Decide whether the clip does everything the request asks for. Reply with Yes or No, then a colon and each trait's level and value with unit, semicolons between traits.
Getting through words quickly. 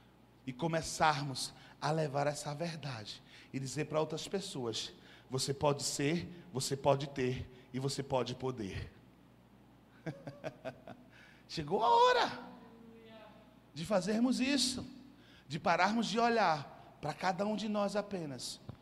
No: slow, 120 wpm